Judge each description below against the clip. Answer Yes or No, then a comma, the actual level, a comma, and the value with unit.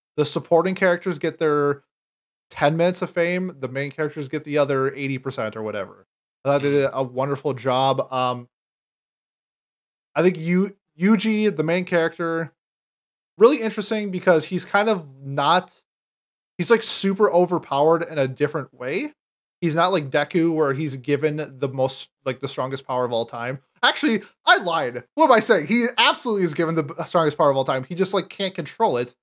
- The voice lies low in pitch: No, medium, 160 Hz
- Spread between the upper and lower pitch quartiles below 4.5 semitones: No, average, 4.9 semitones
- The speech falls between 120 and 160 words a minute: No, average, 180 wpm